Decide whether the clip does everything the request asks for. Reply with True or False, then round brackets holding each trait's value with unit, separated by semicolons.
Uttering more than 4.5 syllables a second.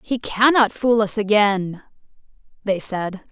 False (3.8 syllables/s)